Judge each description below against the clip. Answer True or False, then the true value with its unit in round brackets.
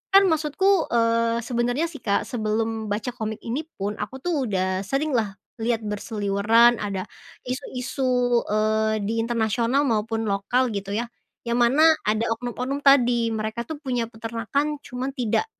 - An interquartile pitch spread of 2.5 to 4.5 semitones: True (2.8 semitones)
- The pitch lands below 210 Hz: False (230 Hz)